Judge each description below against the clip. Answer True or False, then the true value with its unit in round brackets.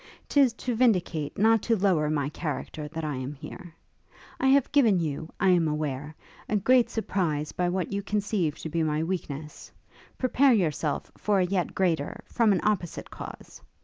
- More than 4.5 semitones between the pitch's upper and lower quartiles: True (5.6 semitones)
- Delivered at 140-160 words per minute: False (175 wpm)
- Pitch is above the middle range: False (180 Hz)